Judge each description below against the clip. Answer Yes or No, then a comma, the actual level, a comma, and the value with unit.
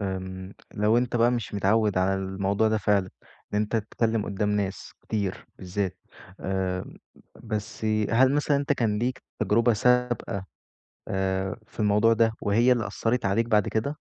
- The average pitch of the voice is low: Yes, low, 105 Hz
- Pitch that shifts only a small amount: No, average, 3.0 semitones